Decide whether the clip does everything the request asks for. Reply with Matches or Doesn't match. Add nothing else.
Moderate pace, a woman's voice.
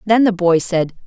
Doesn't match